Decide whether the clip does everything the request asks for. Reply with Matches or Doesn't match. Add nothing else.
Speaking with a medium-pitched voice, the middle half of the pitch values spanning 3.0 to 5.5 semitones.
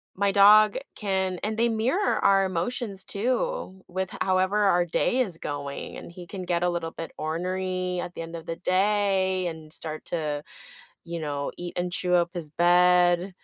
Doesn't match